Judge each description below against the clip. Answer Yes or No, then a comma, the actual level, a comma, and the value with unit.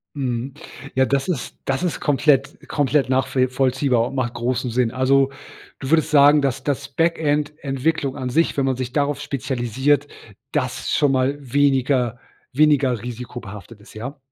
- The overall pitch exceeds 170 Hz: No, low, 135 Hz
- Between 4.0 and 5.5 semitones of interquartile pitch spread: No, narrow, 2.4 semitones